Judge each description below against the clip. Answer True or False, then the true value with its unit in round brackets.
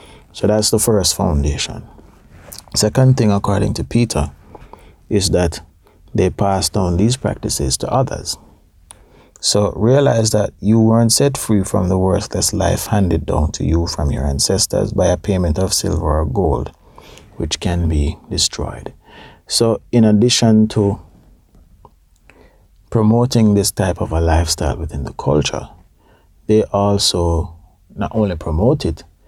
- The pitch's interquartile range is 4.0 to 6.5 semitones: True (4.4 semitones)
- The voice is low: True (100 Hz)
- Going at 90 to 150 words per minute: True (135 wpm)